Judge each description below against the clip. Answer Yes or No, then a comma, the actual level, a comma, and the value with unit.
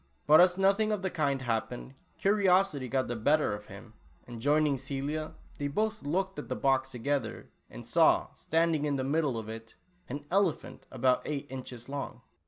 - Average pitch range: Yes, average, 4.6 semitones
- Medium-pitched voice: Yes, medium, 145 Hz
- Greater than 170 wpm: Yes, average, 180 wpm